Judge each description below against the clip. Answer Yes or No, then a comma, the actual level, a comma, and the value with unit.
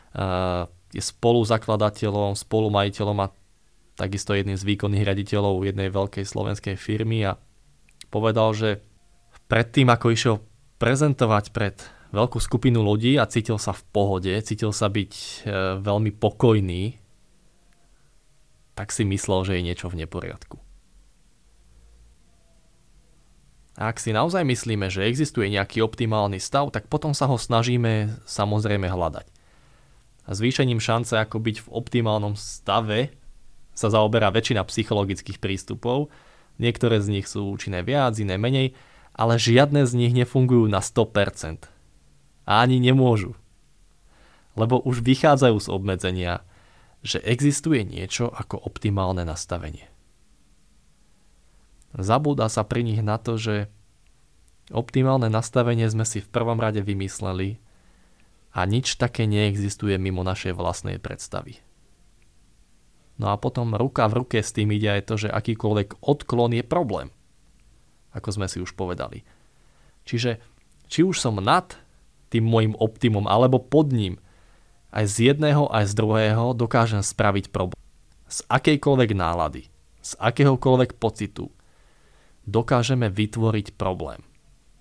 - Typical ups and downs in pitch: Yes, average, 3.4 semitones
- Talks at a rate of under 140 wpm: Yes, average, 125 wpm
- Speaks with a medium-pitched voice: No, low, 110 Hz